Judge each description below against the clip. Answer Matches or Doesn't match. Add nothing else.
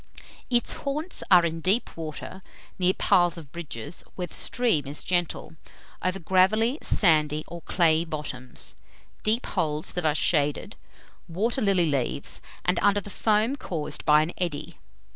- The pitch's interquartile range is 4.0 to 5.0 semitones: Matches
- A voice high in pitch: Doesn't match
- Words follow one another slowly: Doesn't match